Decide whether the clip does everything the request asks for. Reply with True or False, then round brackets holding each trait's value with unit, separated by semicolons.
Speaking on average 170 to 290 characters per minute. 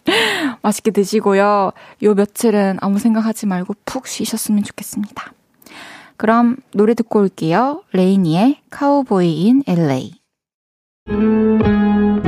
True (240 characters per minute)